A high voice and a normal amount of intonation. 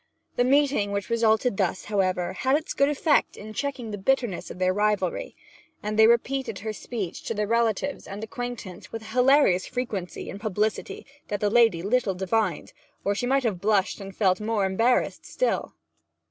Yes: high, 215 Hz; average, 3.9 semitones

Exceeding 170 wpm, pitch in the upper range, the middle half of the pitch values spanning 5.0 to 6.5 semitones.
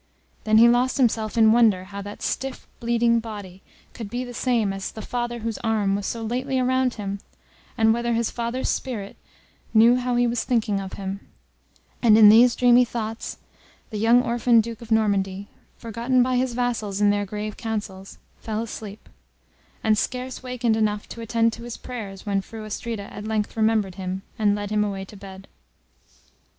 No: average, 180 wpm; high, 225 Hz; narrow, 2.6 semitones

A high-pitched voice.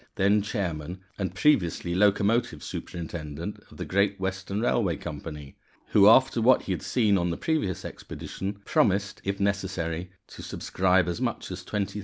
No: very low, 95 Hz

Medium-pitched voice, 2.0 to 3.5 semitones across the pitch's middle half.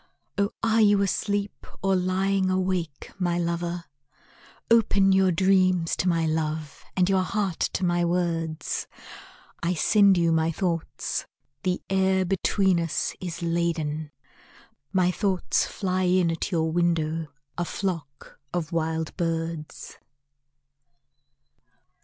Yes: medium, 175 Hz; narrow, 2.5 semitones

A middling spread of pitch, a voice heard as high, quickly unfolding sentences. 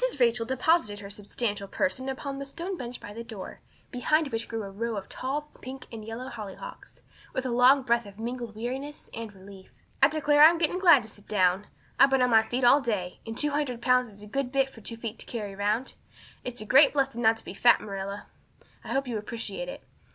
Yes: average, 4.2 semitones; high, 240 Hz; fast, 225 wpm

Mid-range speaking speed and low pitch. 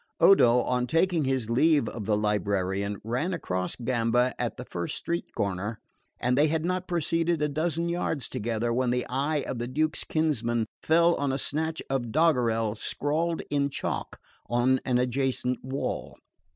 Yes: average, 165 wpm; low, 130 Hz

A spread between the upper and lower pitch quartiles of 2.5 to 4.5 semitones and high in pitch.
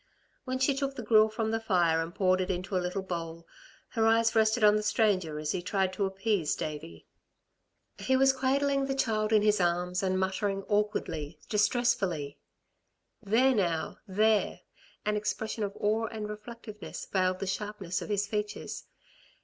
Yes: average, 3.2 semitones; high, 210 Hz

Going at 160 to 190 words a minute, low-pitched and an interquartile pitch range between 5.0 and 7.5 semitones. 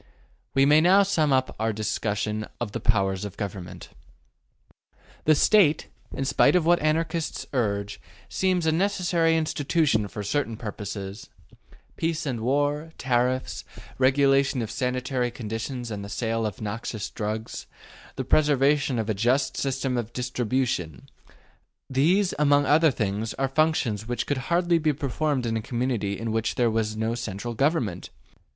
No: average, 145 wpm; low, 125 Hz; average, 5.3 semitones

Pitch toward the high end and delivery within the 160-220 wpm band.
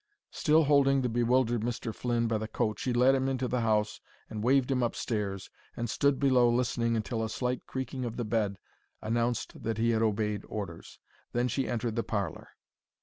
No: low, 120 Hz; average, 190 wpm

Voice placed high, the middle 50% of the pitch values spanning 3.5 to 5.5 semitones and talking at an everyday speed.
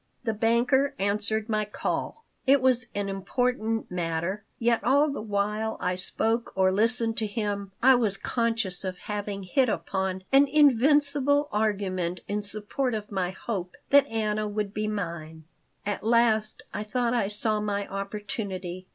No: high, 215 Hz; average, 3.1 semitones; average, 150 wpm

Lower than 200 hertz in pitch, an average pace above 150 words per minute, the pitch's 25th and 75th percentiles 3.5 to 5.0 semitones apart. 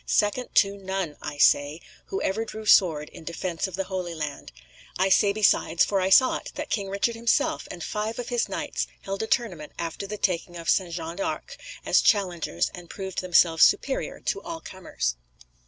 Yes: high, 190 Hz; average, 195 wpm; average, 3.8 semitones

